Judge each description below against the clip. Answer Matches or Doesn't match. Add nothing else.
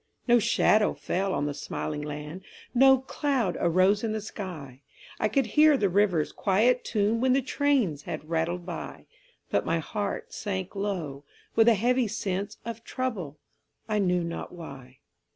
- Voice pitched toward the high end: Matches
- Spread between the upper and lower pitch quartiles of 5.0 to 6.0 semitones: Matches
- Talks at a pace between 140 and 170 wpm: Matches